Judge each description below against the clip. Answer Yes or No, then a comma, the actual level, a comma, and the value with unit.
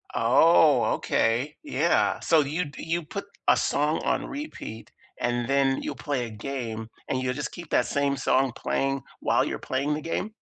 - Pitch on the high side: No, medium, 140 Hz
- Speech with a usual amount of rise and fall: Yes, average, 3.7 semitones